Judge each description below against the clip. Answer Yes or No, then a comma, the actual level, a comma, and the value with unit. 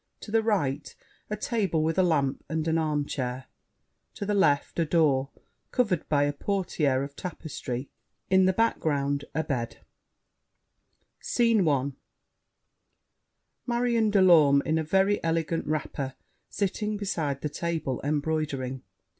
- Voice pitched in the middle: Yes, medium, 160 Hz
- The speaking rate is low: Yes, slow, 130 wpm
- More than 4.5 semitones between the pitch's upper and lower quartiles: Yes, average, 5.2 semitones